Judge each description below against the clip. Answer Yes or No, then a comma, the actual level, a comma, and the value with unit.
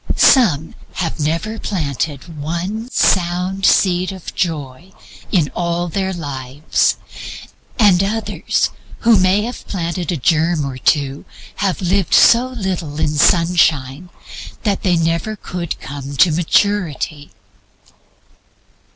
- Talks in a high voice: No, medium, 175 Hz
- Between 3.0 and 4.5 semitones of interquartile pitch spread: Yes, average, 4.0 semitones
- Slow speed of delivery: Yes, slow, 115 wpm